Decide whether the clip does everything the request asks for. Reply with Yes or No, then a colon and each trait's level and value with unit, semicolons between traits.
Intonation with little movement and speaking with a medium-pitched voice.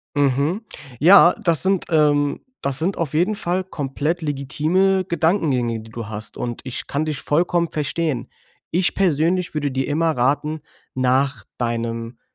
No: average, 4.6 semitones; medium, 150 Hz